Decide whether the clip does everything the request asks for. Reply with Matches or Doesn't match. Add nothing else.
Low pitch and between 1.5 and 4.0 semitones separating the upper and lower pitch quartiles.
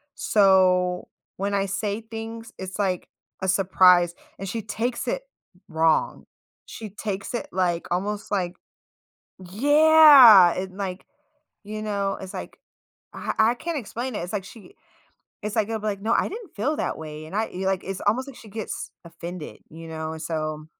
Doesn't match